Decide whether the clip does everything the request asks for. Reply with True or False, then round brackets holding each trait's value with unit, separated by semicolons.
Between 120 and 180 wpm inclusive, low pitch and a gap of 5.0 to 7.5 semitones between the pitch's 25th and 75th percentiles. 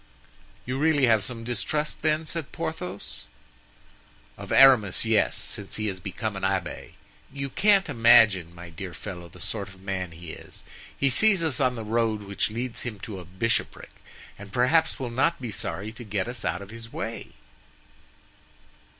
True (170 wpm; 115 Hz; 5.3 semitones)